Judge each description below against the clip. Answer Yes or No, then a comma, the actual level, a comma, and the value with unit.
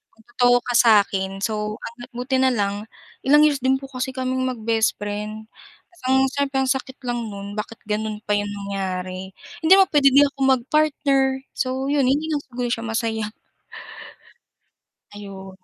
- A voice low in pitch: No, high, 240 Hz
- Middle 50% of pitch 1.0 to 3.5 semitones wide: No, average, 4.2 semitones